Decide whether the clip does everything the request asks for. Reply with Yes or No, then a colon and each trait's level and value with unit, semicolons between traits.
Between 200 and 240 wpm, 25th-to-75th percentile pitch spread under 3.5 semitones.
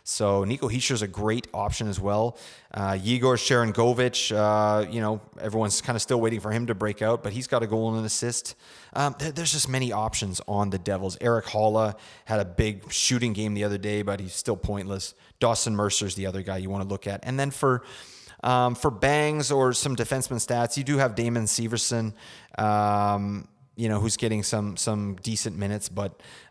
Yes: fast, 205 wpm; average, 3.1 semitones